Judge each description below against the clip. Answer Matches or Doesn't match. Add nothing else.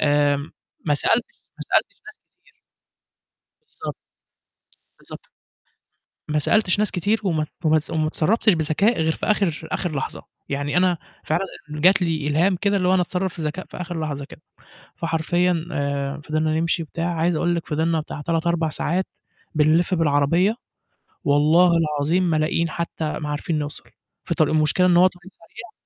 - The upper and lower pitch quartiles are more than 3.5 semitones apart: Doesn't match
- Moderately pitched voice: Matches